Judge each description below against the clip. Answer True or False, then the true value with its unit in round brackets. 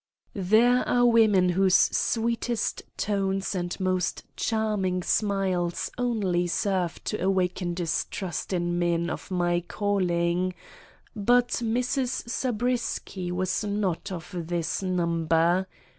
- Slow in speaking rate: True (105 wpm)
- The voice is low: False (185 Hz)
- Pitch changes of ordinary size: True (3.6 semitones)